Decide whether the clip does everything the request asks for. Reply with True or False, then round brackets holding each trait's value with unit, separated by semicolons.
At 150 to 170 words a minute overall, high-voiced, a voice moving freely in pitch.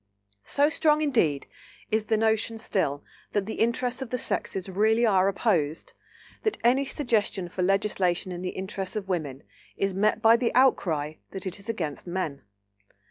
False (165 wpm; 200 Hz; 4.1 semitones)